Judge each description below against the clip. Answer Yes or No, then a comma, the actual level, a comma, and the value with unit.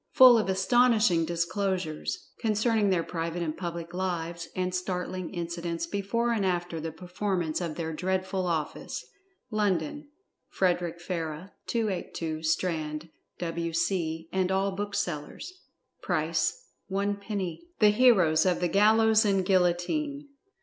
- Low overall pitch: No, medium, 180 Hz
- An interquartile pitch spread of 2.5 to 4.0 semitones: Yes, average, 3.3 semitones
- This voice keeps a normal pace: No, slow, 120 wpm